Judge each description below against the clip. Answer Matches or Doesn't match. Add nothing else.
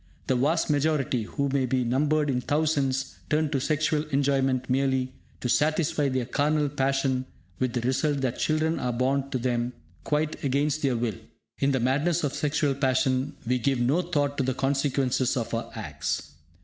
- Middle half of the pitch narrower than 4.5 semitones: Matches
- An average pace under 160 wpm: Doesn't match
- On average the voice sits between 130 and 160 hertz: Matches